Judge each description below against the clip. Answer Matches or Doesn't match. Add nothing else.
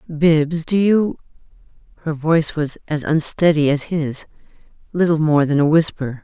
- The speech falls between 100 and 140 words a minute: Matches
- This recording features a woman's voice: Matches